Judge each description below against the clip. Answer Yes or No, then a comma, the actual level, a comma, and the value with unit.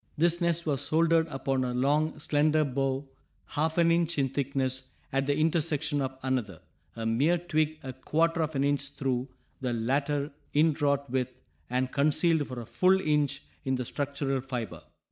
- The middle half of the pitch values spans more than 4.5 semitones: No, average, 3.0 semitones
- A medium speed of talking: Yes, average, 165 wpm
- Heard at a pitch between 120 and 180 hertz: Yes, medium, 140 Hz